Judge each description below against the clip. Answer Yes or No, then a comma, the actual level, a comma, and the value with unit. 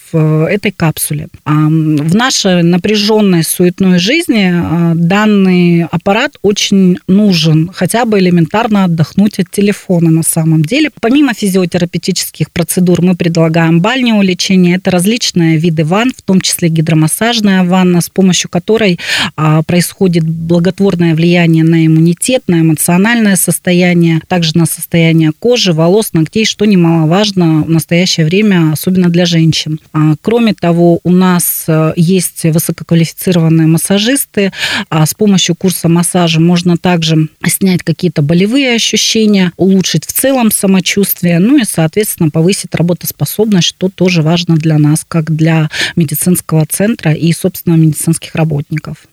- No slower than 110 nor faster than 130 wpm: Yes, average, 125 wpm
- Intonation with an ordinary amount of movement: Yes, average, 3.1 semitones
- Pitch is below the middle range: No, medium, 175 Hz